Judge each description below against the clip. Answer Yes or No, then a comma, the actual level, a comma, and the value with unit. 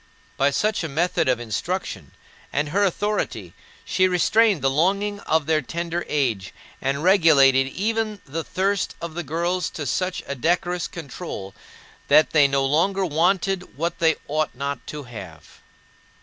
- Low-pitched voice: No, medium, 160 Hz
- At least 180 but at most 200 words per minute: No, average, 150 wpm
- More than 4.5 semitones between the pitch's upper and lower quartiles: Yes, average, 4.9 semitones